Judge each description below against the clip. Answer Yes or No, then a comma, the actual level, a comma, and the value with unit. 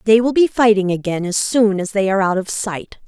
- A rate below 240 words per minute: No, fast, 255 wpm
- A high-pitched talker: Yes, high, 205 Hz